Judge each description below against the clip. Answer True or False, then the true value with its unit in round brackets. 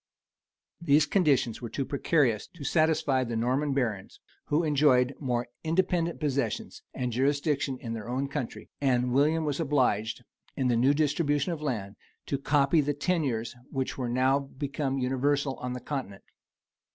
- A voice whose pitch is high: False (135 Hz)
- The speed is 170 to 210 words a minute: False (150 wpm)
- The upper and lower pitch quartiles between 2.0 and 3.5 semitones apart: True (2.9 semitones)